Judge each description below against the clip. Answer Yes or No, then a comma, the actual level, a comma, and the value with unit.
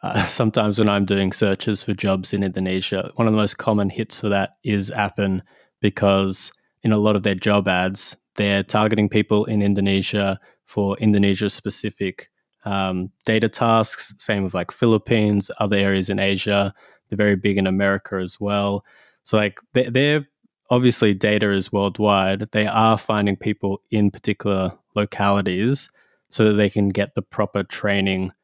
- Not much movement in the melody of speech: Yes, narrow, 1.6 semitones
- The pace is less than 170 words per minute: Yes, average, 160 wpm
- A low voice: Yes, low, 100 Hz